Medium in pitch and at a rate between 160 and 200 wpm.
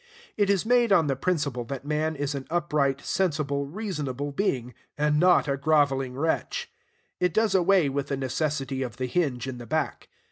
Yes: medium, 145 Hz; average, 180 wpm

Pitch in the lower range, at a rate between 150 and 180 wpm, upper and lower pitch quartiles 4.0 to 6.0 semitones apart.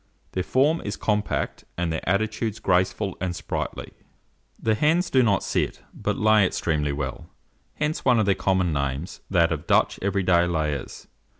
Yes: very low, 95 Hz; average, 165 wpm; average, 4.5 semitones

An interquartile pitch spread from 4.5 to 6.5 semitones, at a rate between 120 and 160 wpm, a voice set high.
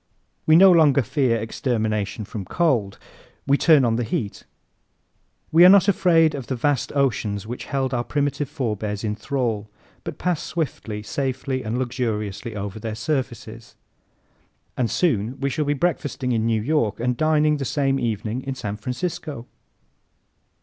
No: average, 4.9 semitones; average, 155 wpm; low, 125 Hz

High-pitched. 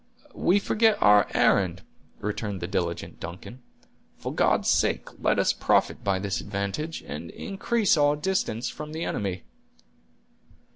No: low, 105 Hz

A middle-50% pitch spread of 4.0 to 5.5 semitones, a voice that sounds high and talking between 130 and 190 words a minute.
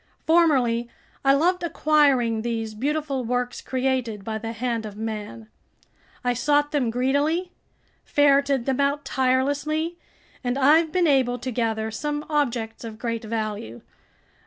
Yes: average, 4.3 semitones; very high, 255 Hz; slow, 135 wpm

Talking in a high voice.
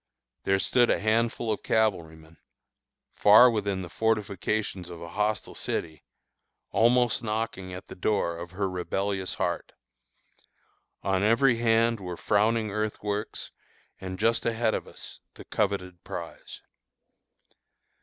No: low, 105 Hz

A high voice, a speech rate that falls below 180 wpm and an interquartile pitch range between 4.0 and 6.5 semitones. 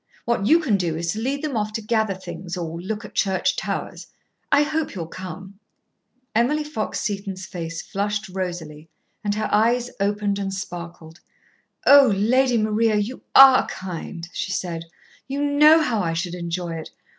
Yes: high, 200 Hz; average, 170 wpm; average, 5.0 semitones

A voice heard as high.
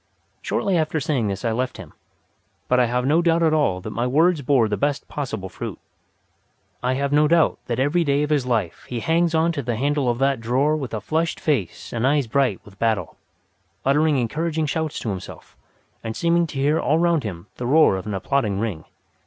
No: low, 135 Hz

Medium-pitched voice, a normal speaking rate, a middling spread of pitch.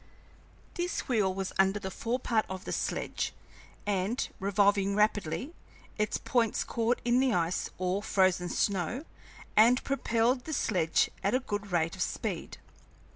No: high, 205 Hz; average, 145 wpm; average, 4.1 semitones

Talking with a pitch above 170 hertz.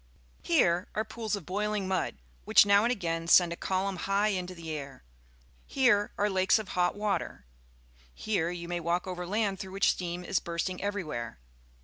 Yes: medium, 185 Hz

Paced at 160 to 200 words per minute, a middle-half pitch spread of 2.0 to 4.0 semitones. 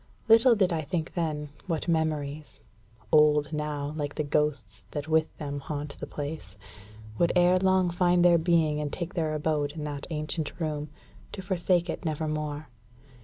Yes: average, 170 wpm; narrow, 2.5 semitones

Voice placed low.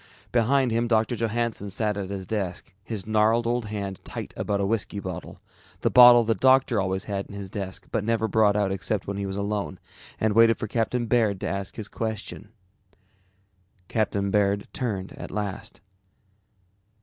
Yes: low, 105 Hz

